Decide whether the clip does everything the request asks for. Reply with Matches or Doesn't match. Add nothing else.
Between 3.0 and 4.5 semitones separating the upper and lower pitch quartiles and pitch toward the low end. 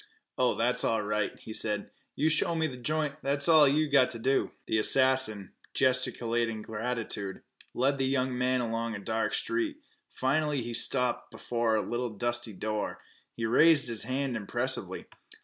Matches